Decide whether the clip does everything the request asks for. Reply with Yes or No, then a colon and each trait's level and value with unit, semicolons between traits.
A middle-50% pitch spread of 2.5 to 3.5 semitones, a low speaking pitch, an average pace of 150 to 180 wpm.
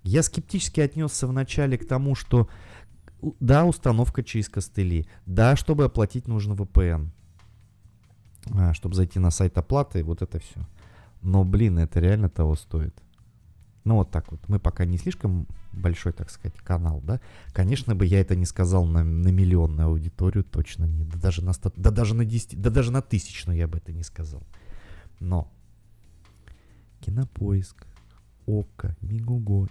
No: average, 4.2 semitones; very low, 95 Hz; fast, 160 wpm